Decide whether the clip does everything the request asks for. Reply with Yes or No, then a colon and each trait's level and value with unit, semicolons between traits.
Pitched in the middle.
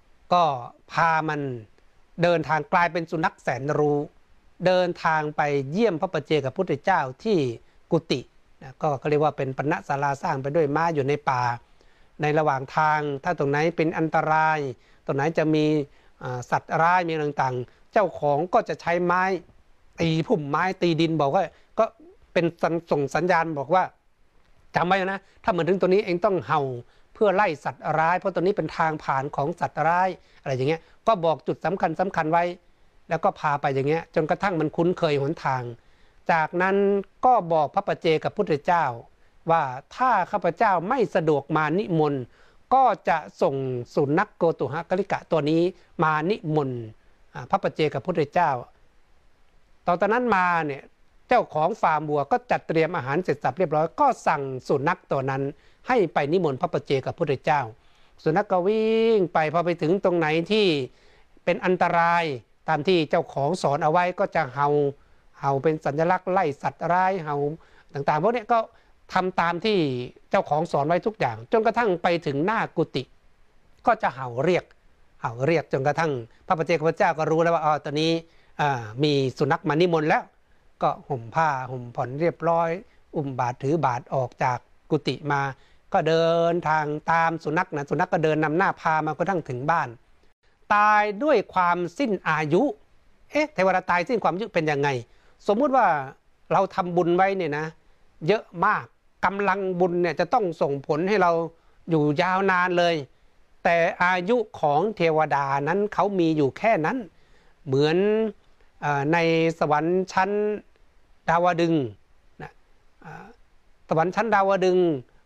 Yes: medium, 165 Hz